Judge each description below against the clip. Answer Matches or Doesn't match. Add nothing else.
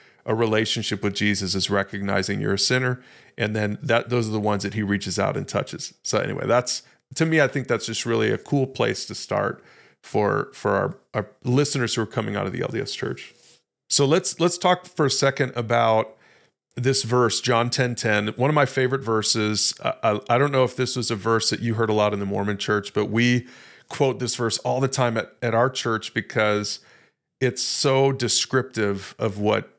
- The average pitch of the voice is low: Matches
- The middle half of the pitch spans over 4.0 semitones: Doesn't match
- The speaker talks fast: Matches